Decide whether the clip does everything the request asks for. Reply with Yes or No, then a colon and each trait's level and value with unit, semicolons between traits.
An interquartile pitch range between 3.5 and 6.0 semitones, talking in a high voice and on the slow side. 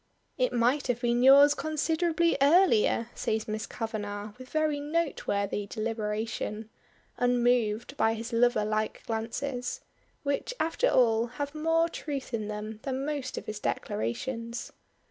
Yes: average, 4.7 semitones; high, 245 Hz; slow, 130 wpm